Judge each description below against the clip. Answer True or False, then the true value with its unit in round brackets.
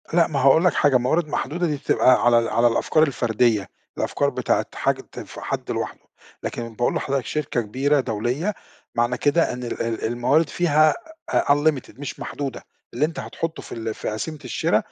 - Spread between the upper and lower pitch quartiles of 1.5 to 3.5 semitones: False (4.5 semitones)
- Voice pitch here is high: False (135 Hz)